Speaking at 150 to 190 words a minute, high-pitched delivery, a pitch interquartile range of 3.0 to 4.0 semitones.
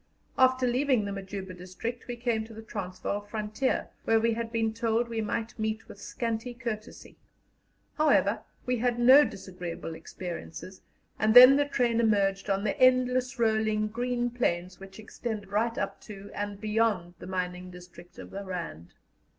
Yes: average, 160 wpm; high, 220 Hz; average, 3.7 semitones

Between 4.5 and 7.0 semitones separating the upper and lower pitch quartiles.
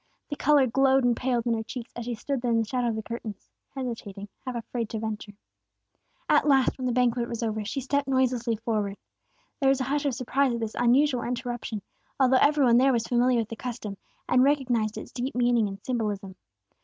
No: narrow, 2.6 semitones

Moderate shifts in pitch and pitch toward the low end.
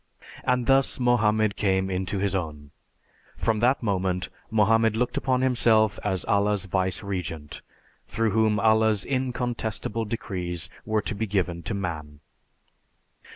Yes: average, 3.3 semitones; low, 105 Hz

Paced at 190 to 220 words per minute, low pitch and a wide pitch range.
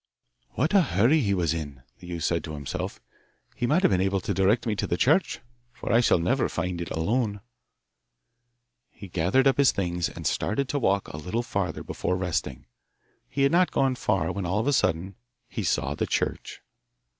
Yes: average, 200 wpm; low, 100 Hz; wide, 6.7 semitones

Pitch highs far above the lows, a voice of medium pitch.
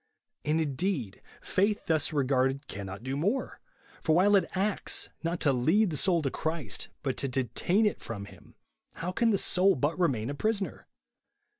Yes: wide, 6.3 semitones; medium, 155 Hz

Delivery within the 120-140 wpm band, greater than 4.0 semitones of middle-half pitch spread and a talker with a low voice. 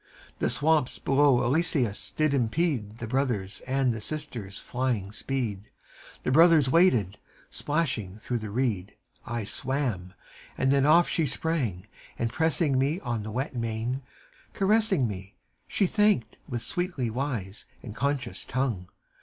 Yes: slow, 135 wpm; average, 5.2 semitones; low, 130 Hz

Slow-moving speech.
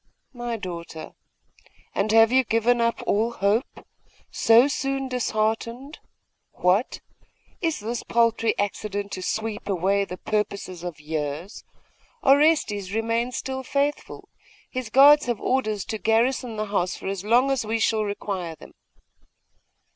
Yes: slow, 130 wpm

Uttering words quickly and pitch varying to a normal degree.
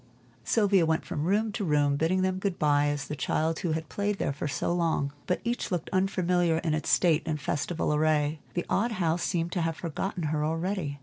Yes: fast, 210 wpm; average, 3.6 semitones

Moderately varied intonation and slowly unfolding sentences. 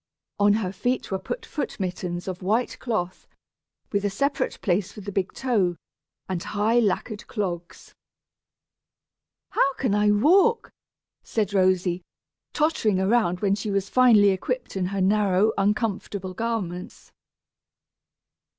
Yes: average, 3.4 semitones; slow, 130 wpm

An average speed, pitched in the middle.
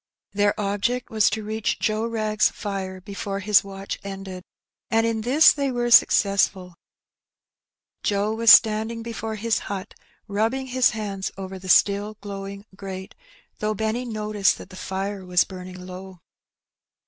No: average, 145 wpm; high, 205 Hz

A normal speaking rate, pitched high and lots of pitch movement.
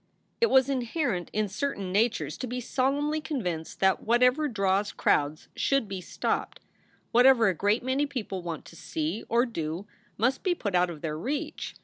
Yes: average, 180 wpm; high, 225 Hz; wide, 6.4 semitones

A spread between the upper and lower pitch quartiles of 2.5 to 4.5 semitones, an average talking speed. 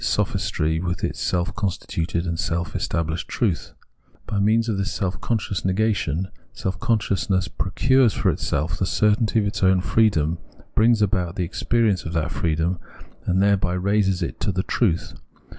Yes: average, 3.6 semitones; average, 160 wpm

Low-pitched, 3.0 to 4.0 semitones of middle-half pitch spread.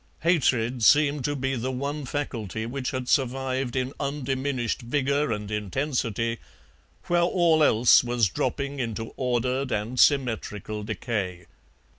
Yes: low, 130 Hz; average, 3.6 semitones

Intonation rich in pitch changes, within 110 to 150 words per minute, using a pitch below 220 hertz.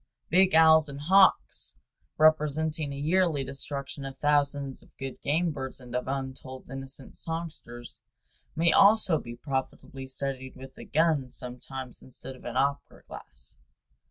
No: average, 3.0 semitones; average, 140 wpm; medium, 140 Hz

